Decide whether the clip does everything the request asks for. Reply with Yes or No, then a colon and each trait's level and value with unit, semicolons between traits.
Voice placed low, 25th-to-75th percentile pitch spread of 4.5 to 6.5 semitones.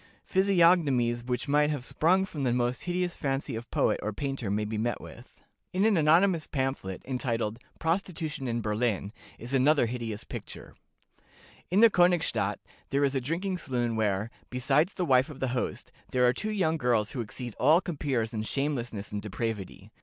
Yes: low, 130 Hz; wide, 5.5 semitones